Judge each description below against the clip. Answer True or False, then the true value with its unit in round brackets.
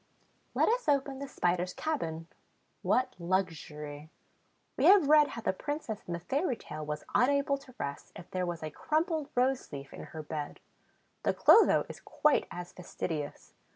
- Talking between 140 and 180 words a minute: True (165 wpm)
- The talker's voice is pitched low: False (190 Hz)